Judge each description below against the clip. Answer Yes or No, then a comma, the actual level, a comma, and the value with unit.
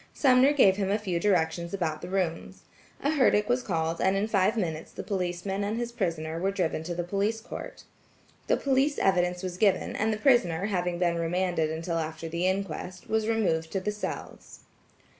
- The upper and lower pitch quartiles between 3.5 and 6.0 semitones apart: Yes, average, 3.8 semitones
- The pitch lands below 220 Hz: Yes, medium, 185 Hz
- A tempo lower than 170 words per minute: No, average, 190 wpm